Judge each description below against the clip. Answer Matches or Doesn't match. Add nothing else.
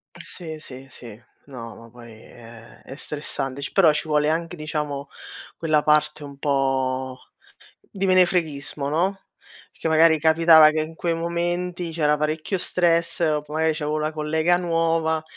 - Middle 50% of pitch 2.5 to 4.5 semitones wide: Matches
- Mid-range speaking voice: Matches